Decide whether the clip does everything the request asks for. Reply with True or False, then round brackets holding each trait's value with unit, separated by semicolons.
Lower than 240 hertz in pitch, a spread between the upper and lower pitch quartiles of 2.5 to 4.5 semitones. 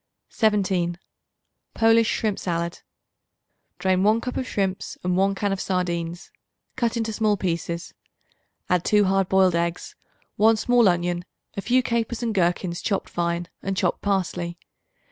True (190 Hz; 3.7 semitones)